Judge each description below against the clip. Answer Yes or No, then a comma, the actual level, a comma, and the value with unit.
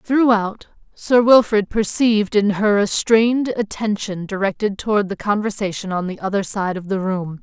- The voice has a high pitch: Yes, high, 205 Hz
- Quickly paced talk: No, average, 160 wpm